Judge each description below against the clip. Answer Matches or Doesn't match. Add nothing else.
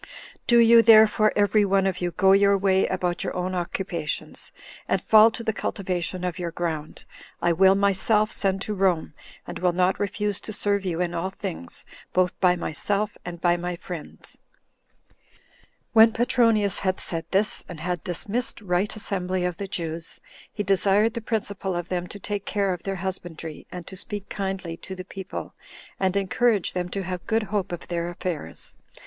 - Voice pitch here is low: Doesn't match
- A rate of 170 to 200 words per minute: Matches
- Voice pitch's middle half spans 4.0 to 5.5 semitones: Doesn't match